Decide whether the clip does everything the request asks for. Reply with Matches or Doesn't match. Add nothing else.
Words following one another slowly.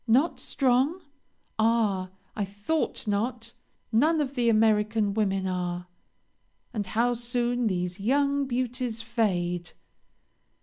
Matches